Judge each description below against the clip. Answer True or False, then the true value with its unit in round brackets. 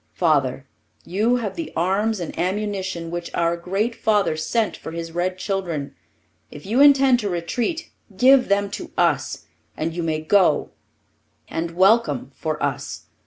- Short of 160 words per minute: True (150 wpm)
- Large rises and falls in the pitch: False (4.7 semitones)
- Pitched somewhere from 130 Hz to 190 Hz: True (185 Hz)